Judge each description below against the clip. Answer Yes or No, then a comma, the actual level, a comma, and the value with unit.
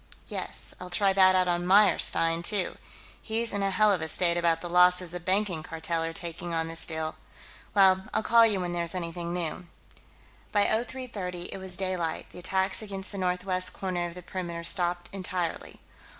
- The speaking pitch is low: No, medium, 180 Hz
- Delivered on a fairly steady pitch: Yes, narrow, 2.1 semitones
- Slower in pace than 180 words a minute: No, average, 185 wpm